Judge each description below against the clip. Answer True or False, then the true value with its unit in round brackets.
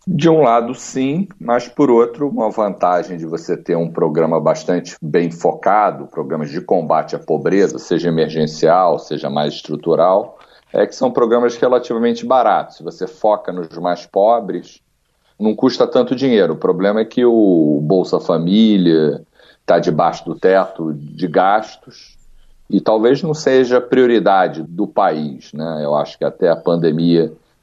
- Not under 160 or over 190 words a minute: False (150 wpm)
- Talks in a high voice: False (105 Hz)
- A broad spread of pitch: True (6.6 semitones)